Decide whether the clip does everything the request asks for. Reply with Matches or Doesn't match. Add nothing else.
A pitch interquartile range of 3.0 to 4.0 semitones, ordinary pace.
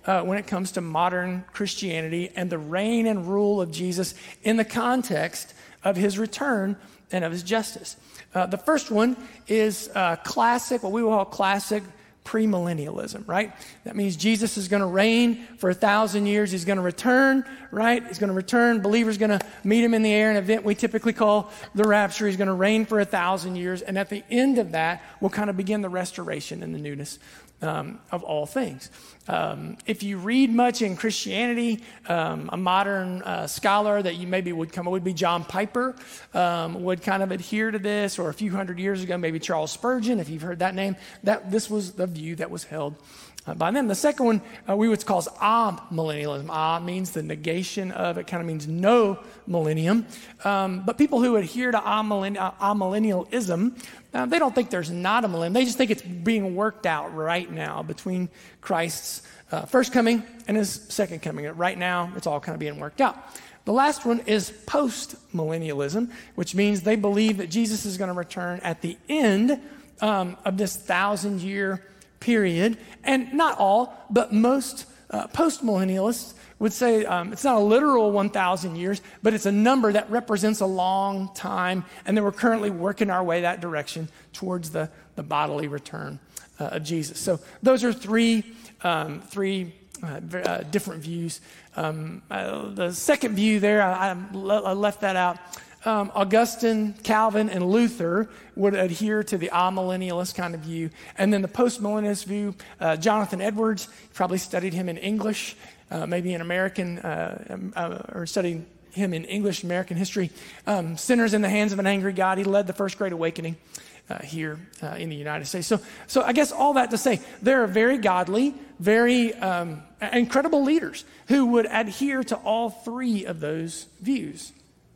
Matches